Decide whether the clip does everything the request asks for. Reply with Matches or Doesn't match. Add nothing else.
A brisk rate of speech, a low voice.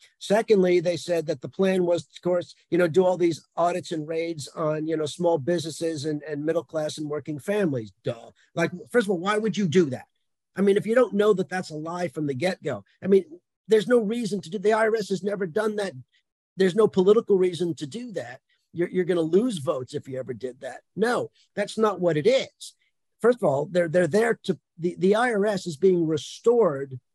Doesn't match